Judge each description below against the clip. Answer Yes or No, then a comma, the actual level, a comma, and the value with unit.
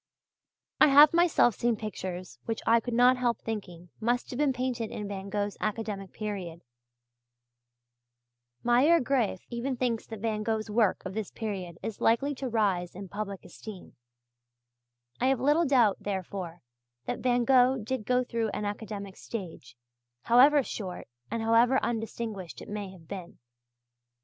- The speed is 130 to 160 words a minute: Yes, average, 150 wpm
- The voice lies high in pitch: Yes, high, 220 Hz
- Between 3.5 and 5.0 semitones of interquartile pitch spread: Yes, average, 3.8 semitones